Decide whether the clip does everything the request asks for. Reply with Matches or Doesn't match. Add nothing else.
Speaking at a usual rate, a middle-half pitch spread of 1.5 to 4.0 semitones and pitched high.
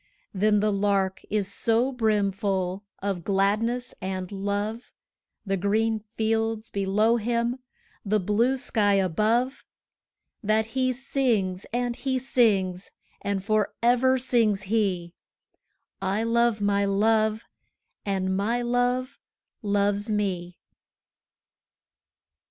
Doesn't match